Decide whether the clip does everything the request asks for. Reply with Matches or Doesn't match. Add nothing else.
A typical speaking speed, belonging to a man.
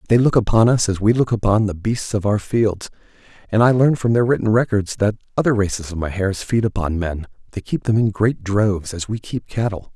Doesn't match